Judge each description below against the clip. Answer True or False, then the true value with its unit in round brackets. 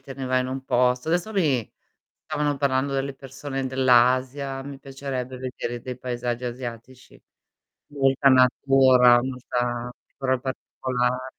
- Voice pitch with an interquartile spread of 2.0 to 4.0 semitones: False (1.4 semitones)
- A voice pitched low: True (130 Hz)